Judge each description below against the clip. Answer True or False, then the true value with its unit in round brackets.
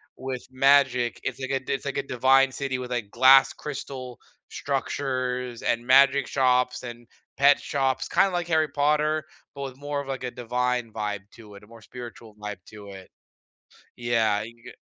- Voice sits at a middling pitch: False (125 Hz)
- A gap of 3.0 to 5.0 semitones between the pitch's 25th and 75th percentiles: False (2.6 semitones)